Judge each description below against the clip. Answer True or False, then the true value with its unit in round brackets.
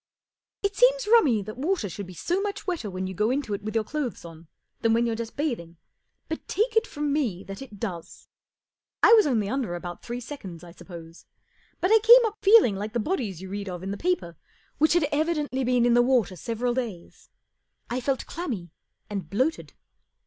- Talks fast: True (215 wpm)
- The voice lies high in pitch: True (240 Hz)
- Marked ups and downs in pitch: True (8.0 semitones)